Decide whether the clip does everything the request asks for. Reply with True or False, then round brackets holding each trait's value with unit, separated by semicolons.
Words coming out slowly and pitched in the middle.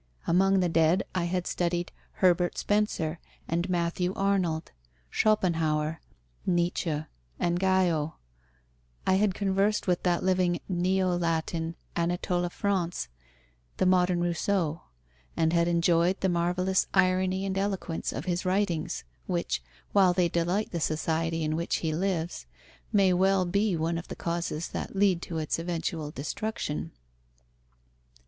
True (130 wpm; 175 Hz)